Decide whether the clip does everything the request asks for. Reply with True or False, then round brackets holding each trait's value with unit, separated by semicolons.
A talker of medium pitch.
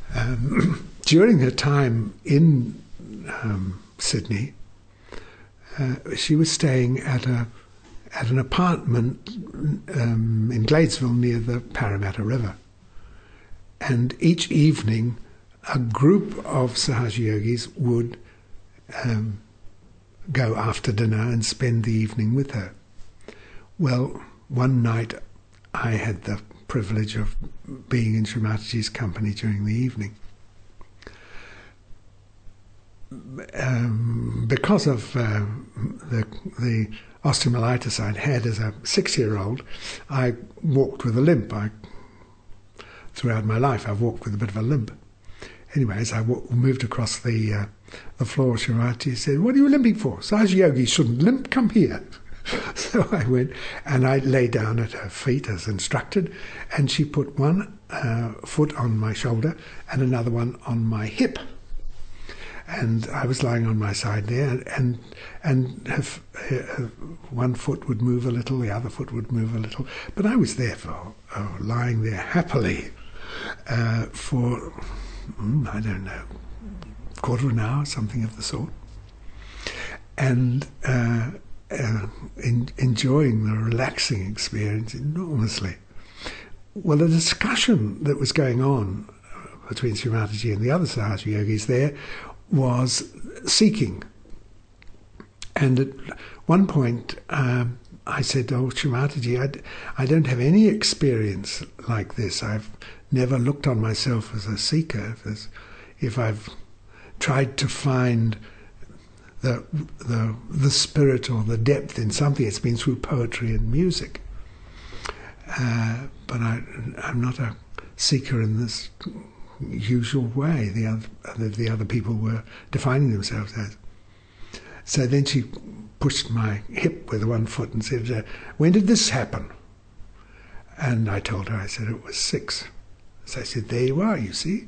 False (120 Hz)